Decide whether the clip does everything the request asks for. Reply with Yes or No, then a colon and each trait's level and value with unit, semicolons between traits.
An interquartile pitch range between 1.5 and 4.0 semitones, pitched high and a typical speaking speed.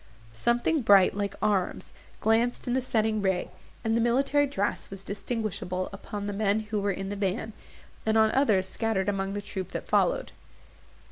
Yes: narrow, 2.6 semitones; high, 210 Hz; average, 175 wpm